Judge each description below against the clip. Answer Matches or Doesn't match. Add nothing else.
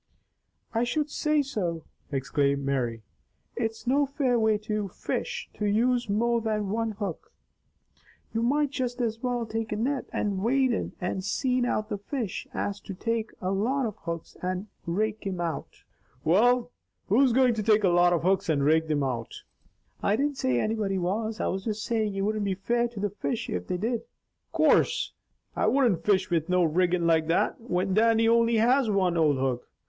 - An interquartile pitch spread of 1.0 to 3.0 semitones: Doesn't match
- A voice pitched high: Matches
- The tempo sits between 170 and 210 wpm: Matches